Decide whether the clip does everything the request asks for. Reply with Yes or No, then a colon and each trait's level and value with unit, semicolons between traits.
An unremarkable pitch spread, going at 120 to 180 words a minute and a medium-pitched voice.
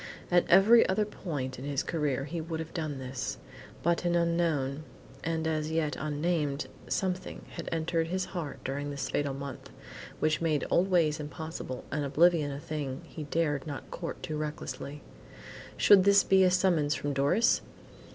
Yes: average, 3.2 semitones; average, 165 wpm; medium, 155 Hz